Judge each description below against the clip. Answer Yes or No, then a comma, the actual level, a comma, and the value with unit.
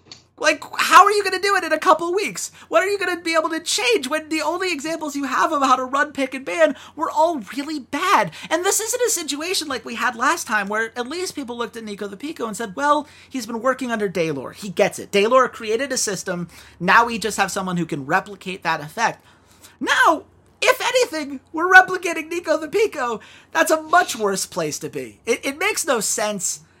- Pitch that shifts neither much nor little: No, wide, 7.2 semitones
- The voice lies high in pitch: Yes, very high, 280 Hz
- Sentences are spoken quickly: Yes, fast, 230 wpm